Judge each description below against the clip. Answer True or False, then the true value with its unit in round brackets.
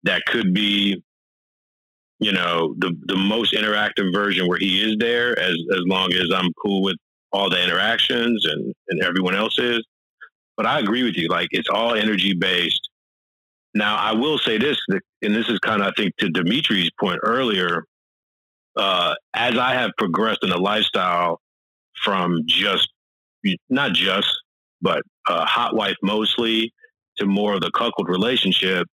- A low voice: True (100 Hz)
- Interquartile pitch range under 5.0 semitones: True (2.9 semitones)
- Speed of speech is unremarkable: True (160 wpm)